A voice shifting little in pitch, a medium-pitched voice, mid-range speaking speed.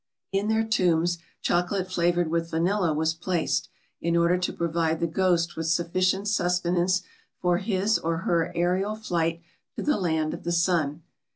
Yes: narrow, 1.8 semitones; medium, 175 Hz; average, 160 wpm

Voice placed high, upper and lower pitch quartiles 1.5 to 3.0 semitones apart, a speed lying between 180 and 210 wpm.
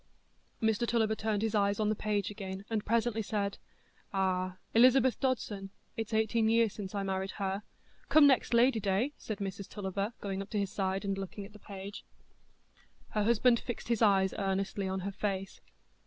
No: high, 205 Hz; narrow, 2.4 semitones; average, 170 wpm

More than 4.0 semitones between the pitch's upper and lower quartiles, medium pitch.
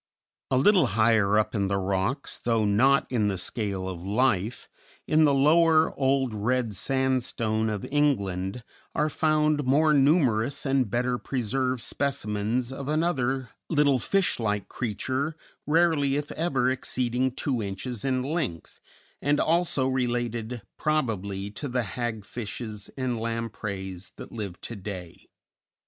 No: average, 4.7 semitones; low, 125 Hz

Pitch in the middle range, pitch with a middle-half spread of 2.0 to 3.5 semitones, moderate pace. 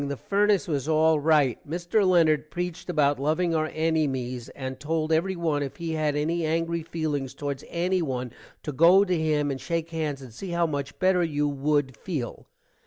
Yes: medium, 155 Hz; average, 2.9 semitones; average, 180 wpm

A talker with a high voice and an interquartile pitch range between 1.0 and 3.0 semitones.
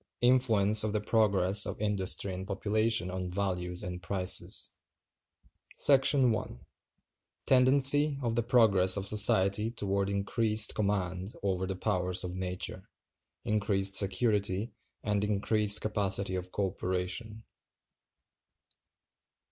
No: low, 100 Hz; average, 2.7 semitones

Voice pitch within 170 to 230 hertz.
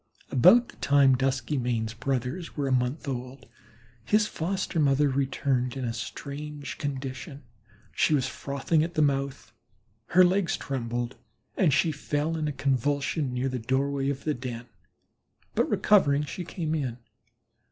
No: medium, 140 Hz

